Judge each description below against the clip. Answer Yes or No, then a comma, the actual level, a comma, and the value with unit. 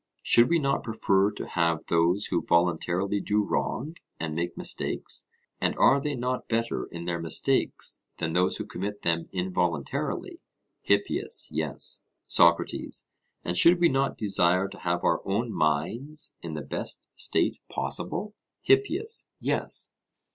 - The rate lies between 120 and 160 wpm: Yes, average, 140 wpm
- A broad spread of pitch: Yes, wide, 6.7 semitones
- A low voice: Yes, very low, 95 Hz